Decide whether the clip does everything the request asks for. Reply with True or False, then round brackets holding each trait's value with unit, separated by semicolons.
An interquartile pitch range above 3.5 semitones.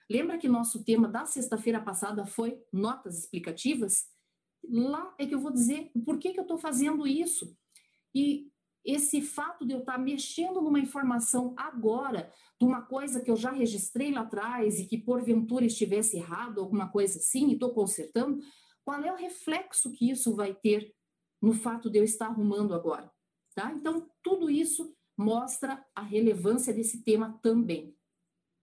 True (4.9 semitones)